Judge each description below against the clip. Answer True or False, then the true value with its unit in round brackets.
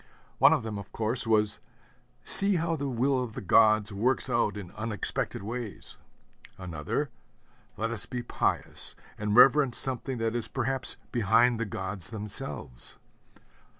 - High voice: False (115 Hz)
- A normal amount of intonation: True (3.3 semitones)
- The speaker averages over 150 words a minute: False (145 wpm)